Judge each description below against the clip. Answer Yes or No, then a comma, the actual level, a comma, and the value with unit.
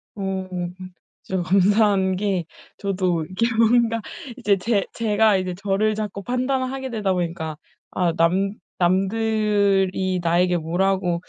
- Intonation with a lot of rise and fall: No, average, 2.9 semitones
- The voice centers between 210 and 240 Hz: No, high, 195 Hz